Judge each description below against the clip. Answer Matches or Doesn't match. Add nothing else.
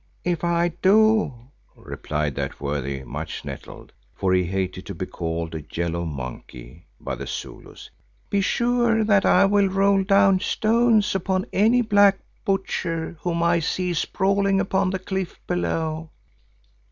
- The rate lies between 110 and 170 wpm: Matches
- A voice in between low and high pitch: Matches